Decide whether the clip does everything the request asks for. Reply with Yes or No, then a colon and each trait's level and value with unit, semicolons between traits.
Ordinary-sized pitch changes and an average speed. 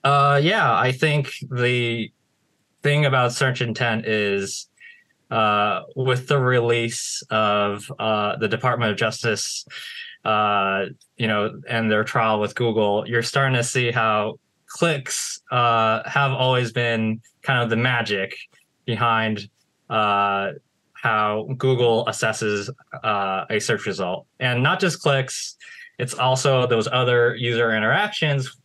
No: average, 3.1 semitones; slow, 130 wpm